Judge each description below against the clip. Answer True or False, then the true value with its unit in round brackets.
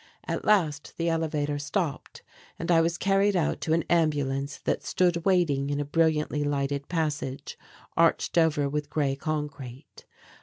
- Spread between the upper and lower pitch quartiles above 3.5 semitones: False (2.6 semitones)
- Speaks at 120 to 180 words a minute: True (150 wpm)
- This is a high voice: False (150 Hz)